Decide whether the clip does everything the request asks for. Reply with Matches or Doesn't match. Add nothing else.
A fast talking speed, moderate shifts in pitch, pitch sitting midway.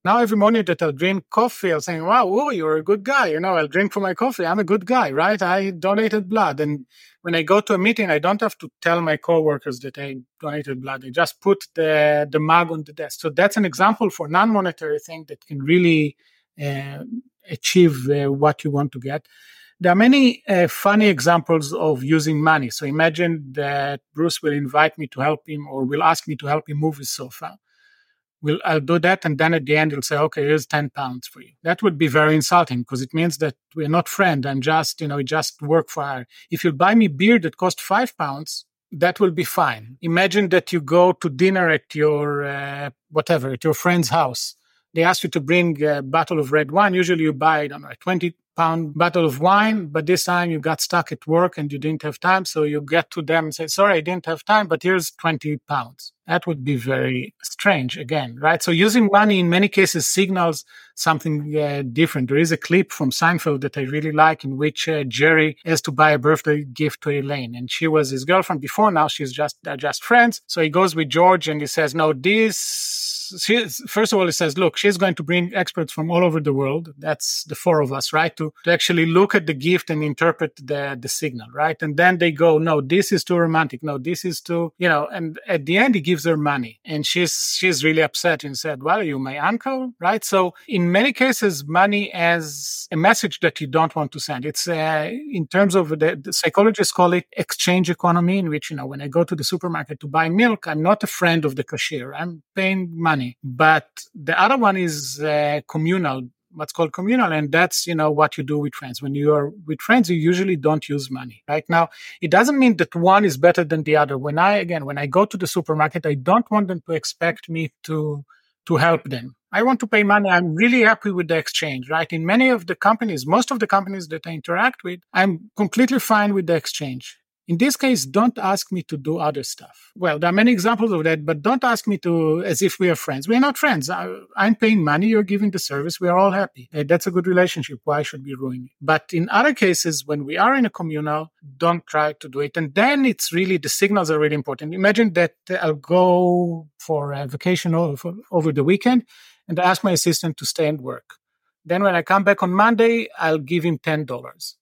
Matches